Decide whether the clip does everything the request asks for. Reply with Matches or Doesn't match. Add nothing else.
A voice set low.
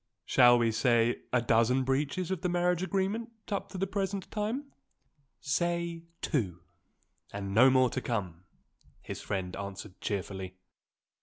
Matches